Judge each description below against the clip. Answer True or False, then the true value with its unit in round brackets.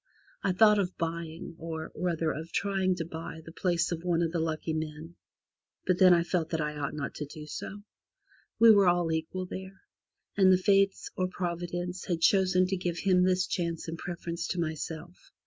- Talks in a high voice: False (175 Hz)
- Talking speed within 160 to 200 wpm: True (195 wpm)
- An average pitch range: False (2.2 semitones)